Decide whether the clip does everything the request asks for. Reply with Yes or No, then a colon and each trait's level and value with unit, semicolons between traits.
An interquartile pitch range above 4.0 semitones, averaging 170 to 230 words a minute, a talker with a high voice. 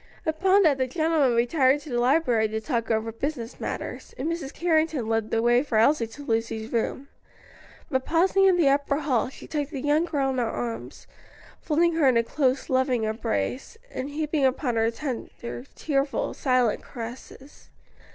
Yes: average, 4.6 semitones; average, 175 wpm; very high, 265 Hz